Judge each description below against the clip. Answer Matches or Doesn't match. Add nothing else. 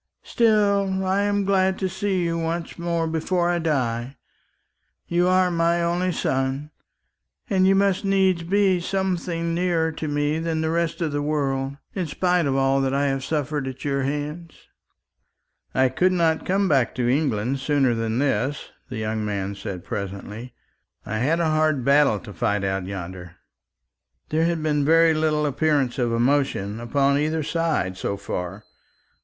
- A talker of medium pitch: Matches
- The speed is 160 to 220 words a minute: Matches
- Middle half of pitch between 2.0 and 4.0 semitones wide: Doesn't match